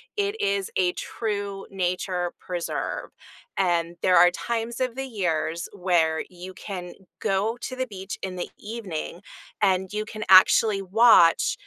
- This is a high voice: Yes, high, 195 Hz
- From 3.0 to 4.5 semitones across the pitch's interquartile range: Yes, average, 3.7 semitones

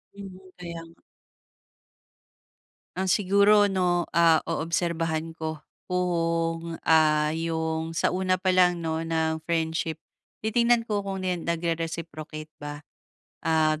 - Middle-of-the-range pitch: Yes, medium, 165 Hz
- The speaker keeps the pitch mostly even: Yes, narrow, 2.2 semitones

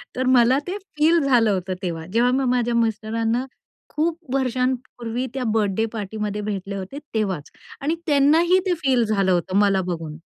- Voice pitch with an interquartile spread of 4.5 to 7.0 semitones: Yes, average, 4.9 semitones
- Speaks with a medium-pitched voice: No, high, 230 Hz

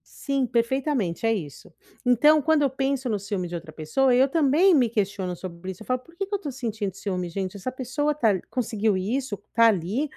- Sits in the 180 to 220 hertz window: No, high, 235 Hz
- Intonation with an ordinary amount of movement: No, wide, 6.1 semitones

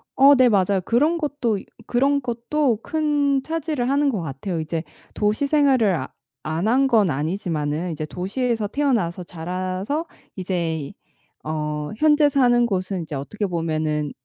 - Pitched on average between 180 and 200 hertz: No, high, 210 Hz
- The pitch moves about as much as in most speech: No, wide, 8.5 semitones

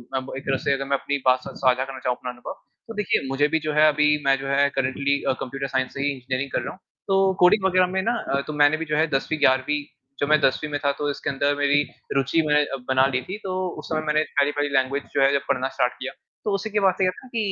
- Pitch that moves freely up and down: No, narrow, 2.5 semitones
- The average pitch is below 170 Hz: Yes, medium, 140 Hz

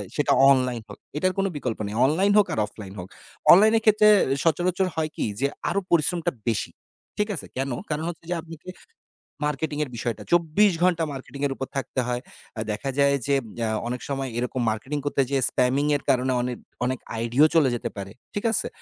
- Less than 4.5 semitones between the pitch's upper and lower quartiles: No, average, 5.2 semitones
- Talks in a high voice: No, medium, 140 Hz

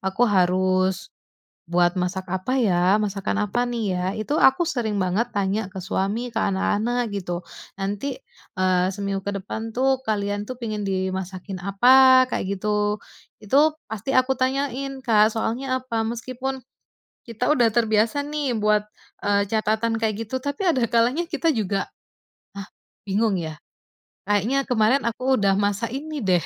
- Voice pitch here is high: Yes, high, 215 Hz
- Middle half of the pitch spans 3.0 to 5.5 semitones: Yes, average, 4.5 semitones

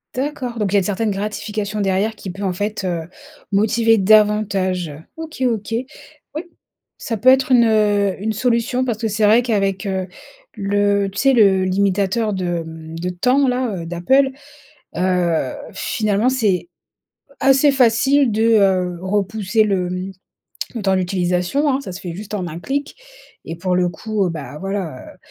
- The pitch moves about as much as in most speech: Yes, average, 3.6 semitones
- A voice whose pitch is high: Yes, high, 205 Hz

